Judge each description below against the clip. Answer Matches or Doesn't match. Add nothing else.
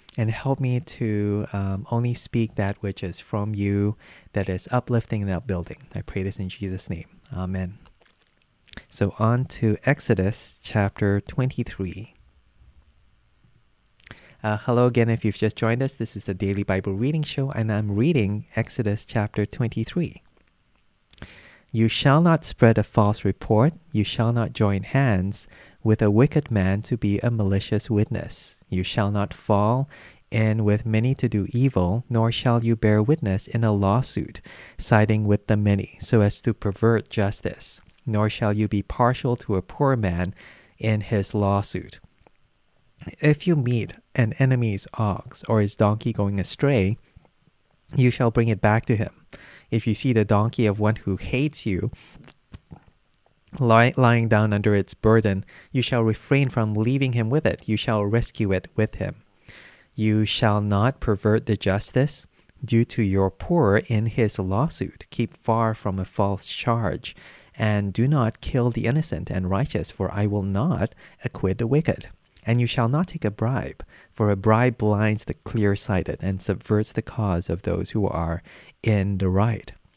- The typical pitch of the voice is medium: Doesn't match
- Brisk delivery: Doesn't match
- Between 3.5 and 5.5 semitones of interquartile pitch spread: Doesn't match